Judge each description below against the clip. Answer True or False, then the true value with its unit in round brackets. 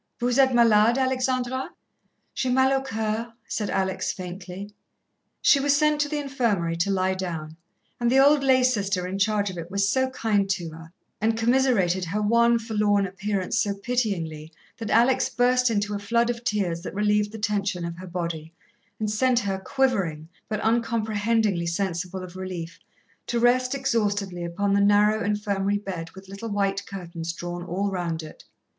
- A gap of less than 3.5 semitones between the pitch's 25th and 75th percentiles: False (4.2 semitones)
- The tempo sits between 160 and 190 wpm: True (170 wpm)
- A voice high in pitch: True (205 Hz)